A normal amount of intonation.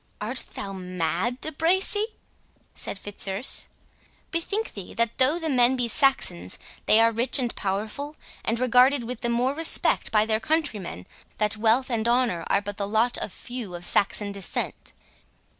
Yes: average, 4.4 semitones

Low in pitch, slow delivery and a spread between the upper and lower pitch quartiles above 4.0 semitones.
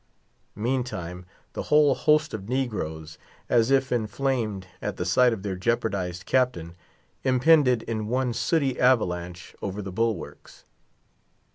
Yes: low, 115 Hz; slow, 125 wpm; wide, 5.6 semitones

